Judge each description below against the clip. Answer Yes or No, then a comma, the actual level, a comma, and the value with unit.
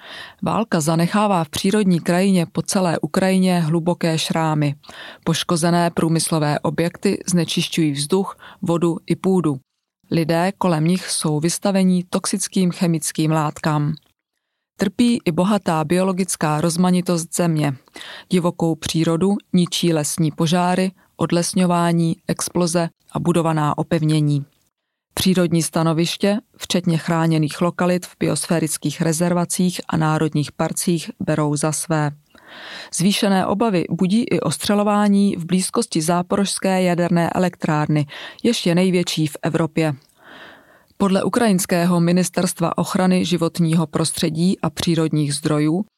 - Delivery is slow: Yes, slow, 105 wpm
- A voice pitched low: No, medium, 170 Hz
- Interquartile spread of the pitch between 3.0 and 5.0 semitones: No, narrow, 2.4 semitones